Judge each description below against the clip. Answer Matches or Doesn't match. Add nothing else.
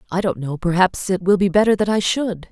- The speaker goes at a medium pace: Doesn't match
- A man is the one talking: Doesn't match